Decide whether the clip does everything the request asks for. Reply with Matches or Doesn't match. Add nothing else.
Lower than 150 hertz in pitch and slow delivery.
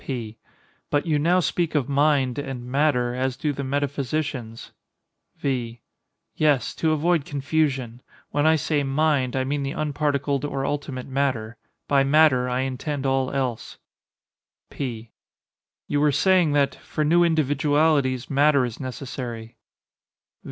Matches